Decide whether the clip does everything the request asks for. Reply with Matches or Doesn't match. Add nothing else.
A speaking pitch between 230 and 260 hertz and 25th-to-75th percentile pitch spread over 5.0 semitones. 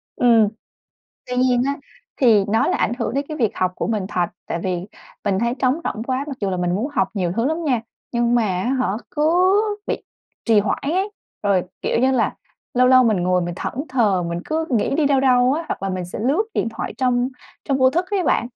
Matches